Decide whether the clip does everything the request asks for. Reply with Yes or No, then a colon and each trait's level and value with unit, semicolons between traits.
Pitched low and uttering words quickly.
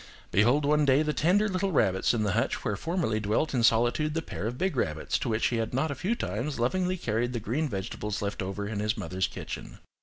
Yes: low, 120 Hz; fast, 235 wpm